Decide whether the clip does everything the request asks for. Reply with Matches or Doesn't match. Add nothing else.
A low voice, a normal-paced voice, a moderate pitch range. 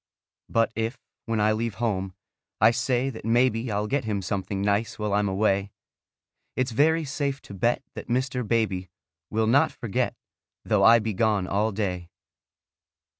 Matches